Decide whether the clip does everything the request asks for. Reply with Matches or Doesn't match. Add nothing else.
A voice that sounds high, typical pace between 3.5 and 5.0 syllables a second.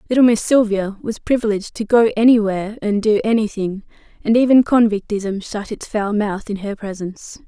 Doesn't match